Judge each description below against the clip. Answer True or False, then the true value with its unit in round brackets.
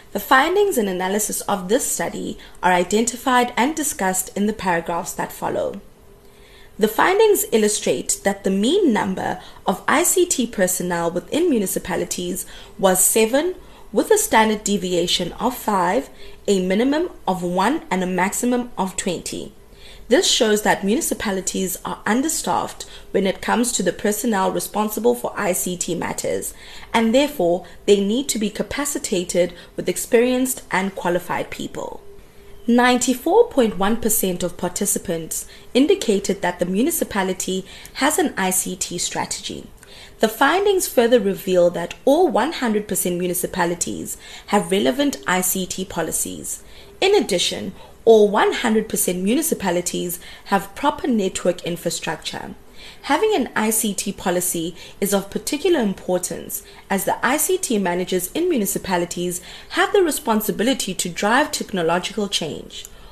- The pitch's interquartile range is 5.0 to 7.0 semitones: True (5.3 semitones)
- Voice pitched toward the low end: False (205 Hz)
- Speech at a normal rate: False (120 wpm)